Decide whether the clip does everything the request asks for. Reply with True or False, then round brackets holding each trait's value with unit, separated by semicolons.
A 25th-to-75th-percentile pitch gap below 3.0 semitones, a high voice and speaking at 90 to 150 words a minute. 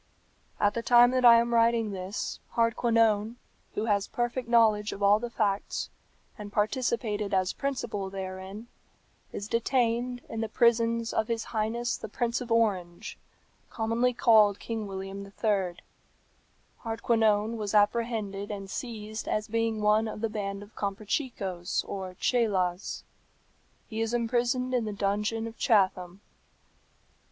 True (2.5 semitones; 220 Hz; 135 wpm)